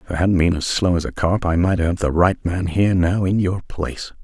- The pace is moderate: No, fast, 285 wpm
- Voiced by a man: Yes, male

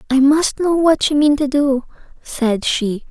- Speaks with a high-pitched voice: Yes, very high, 275 Hz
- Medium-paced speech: Yes, average, 195 wpm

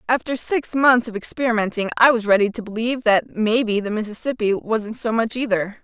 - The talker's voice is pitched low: No, high, 225 Hz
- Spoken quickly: No, average, 185 wpm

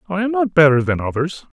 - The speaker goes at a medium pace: No, fast, 225 wpm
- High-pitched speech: No, medium, 170 Hz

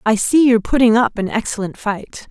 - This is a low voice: No, high, 225 Hz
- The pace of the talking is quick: Yes, fast, 210 wpm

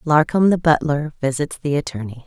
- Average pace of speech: Yes, average, 160 wpm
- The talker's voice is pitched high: No, medium, 145 Hz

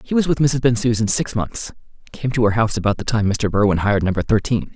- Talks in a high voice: No, low, 110 Hz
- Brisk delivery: Yes, fast, 240 wpm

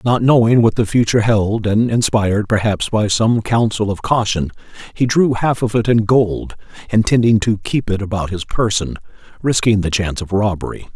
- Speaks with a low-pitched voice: Yes, low, 110 Hz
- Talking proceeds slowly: No, average, 180 wpm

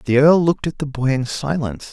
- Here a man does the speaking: Yes, male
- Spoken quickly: Yes, fast, 250 wpm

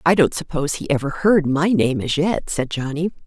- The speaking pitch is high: No, medium, 155 Hz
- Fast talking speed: Yes, fast, 220 wpm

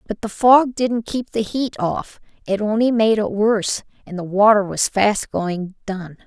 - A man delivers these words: No, female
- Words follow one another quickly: No, average, 190 wpm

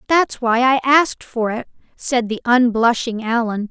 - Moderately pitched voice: No, high, 240 Hz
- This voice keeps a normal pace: Yes, average, 160 wpm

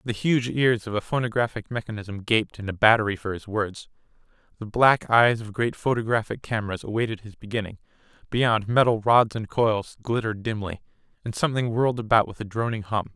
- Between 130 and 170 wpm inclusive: No, average, 180 wpm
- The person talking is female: No, male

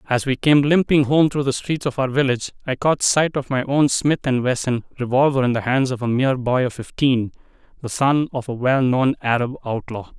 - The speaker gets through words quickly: Yes, fast, 210 wpm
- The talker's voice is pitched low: Yes, low, 130 Hz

